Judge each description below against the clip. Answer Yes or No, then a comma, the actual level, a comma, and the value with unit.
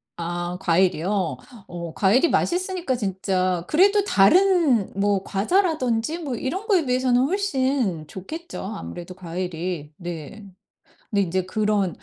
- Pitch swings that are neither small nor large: No, wide, 8.8 semitones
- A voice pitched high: Yes, high, 205 Hz